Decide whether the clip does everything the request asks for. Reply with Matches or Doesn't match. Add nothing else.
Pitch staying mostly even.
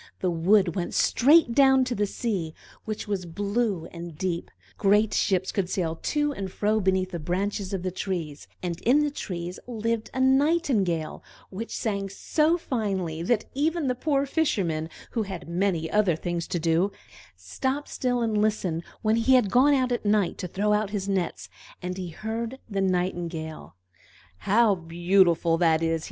Doesn't match